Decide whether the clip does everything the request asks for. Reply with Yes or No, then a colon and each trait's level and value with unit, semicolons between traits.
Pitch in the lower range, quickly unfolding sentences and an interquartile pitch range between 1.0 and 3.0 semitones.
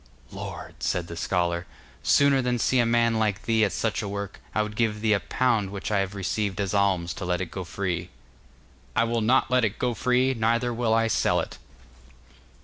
No: low, 105 Hz; fast, 210 wpm; average, 3.4 semitones